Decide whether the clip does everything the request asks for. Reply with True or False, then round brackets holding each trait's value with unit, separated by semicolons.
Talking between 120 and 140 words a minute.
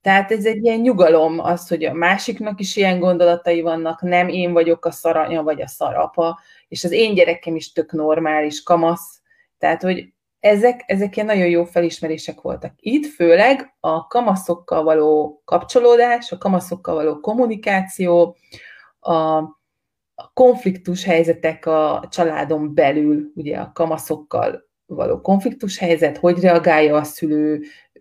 True (135 wpm)